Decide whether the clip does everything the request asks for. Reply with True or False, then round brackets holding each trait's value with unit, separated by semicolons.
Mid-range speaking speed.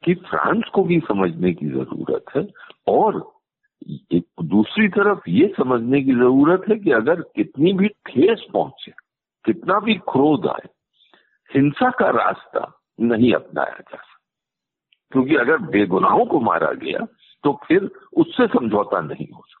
True (140 wpm)